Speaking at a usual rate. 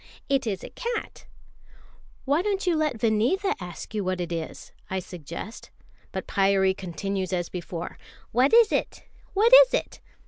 Yes: average, 160 wpm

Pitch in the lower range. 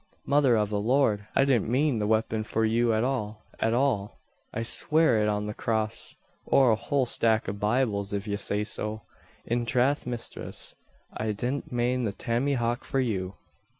Yes: low, 115 Hz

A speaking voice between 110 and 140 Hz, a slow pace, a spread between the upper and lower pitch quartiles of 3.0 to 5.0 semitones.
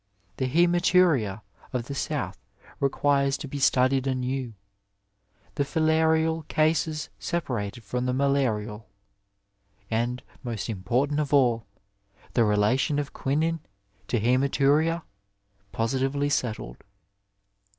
Yes: low, 135 Hz; slow, 105 wpm; average, 4.2 semitones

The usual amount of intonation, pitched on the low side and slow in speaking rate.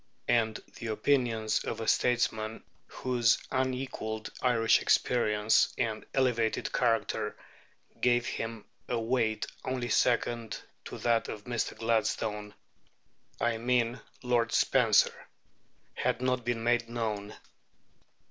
No: narrow, 1.9 semitones; low, 115 Hz; slow, 110 wpm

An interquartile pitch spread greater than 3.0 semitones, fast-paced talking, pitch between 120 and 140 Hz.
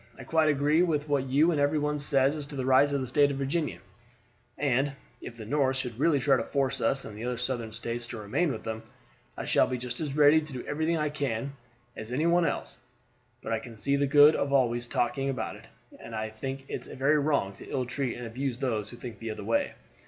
Yes: average, 3.4 semitones; fast, 240 wpm; low, 135 Hz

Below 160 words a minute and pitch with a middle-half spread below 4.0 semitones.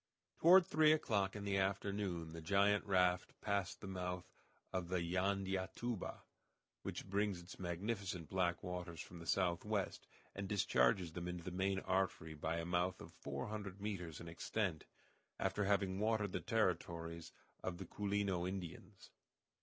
Yes: average, 150 wpm; narrow, 2.5 semitones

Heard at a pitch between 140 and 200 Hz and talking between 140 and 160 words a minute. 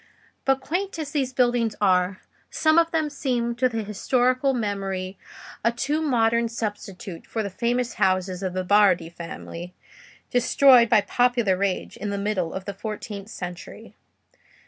No: high, 220 Hz; average, 150 wpm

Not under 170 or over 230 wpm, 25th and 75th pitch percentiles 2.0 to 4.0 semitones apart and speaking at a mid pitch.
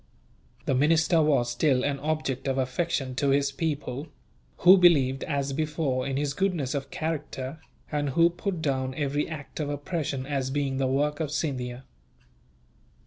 No: average, 155 wpm; average, 2.8 semitones; medium, 145 Hz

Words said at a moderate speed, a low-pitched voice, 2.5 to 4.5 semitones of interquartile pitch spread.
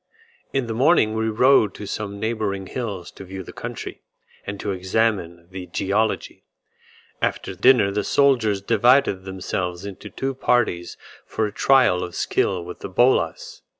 Yes: average, 150 wpm; low, 105 Hz; average, 4.2 semitones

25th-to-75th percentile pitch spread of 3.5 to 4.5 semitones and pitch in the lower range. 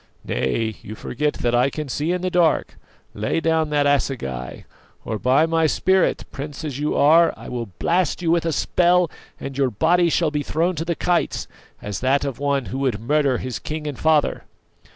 No: average, 4.2 semitones; medium, 150 Hz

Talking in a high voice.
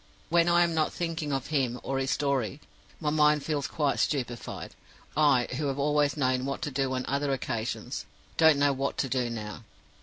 No: medium, 140 Hz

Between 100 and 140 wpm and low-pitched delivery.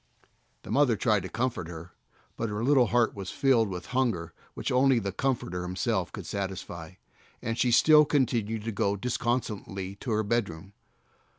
No: average, 165 wpm; low, 110 Hz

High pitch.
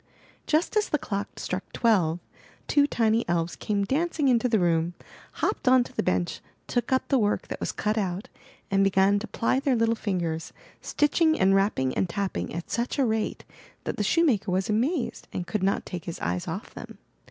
Yes: high, 210 Hz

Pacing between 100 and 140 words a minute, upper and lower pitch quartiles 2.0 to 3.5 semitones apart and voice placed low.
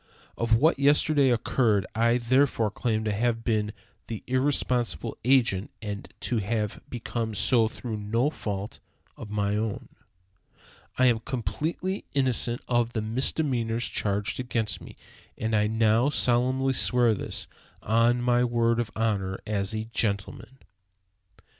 Yes: slow, 135 wpm; narrow, 2.5 semitones; low, 115 Hz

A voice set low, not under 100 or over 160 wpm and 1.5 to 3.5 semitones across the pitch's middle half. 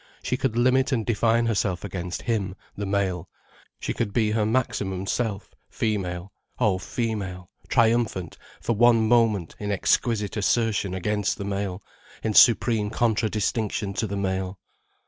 Yes: low, 105 Hz; average, 140 wpm; average, 3.0 semitones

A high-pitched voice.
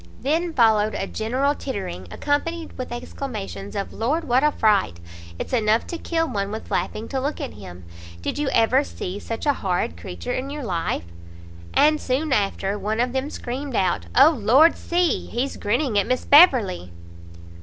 Yes: high, 245 Hz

